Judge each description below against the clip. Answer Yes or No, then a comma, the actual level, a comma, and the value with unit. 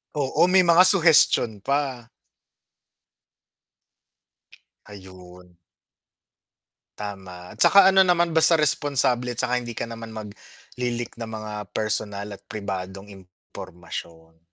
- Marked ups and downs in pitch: Yes, wide, 6.7 semitones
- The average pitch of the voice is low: Yes, low, 110 Hz